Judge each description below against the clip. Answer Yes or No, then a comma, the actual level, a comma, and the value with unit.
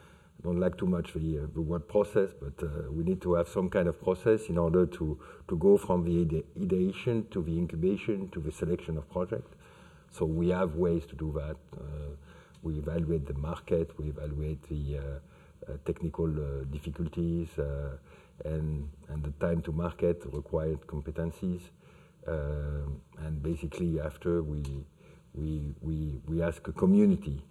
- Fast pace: No, average, 165 wpm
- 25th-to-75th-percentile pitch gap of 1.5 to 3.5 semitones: Yes, narrow, 2.6 semitones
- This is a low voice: Yes, very low, 80 Hz